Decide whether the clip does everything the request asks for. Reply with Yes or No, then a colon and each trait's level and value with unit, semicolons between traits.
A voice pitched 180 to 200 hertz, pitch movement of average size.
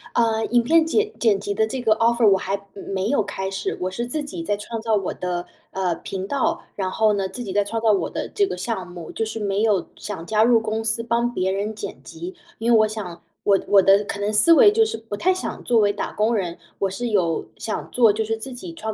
No: high, 215 Hz; average, 3.0 semitones